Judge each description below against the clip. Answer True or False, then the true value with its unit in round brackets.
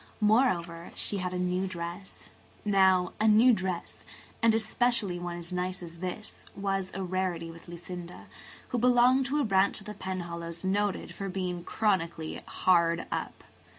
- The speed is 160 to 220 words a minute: False (150 wpm)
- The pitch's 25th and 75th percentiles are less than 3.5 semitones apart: True (3.0 semitones)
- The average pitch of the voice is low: False (185 Hz)